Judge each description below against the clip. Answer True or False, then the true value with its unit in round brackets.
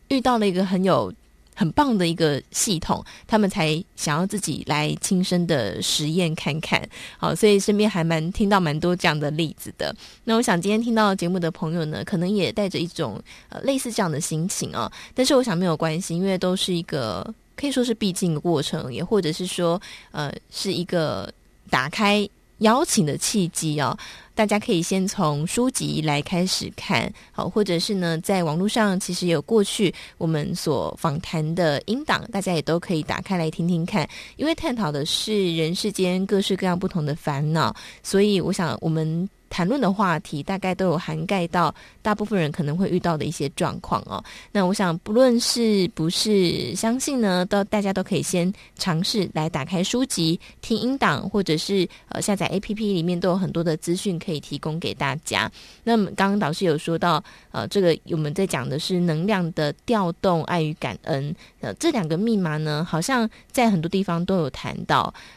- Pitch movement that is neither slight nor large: True (3.9 semitones)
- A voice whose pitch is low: False (180 Hz)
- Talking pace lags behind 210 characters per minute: False (285 characters per minute)